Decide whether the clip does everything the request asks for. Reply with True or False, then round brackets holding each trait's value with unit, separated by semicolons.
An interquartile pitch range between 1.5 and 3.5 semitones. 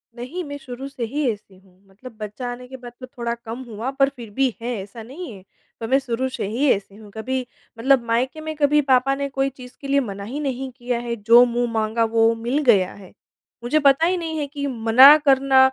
True (3.2 semitones)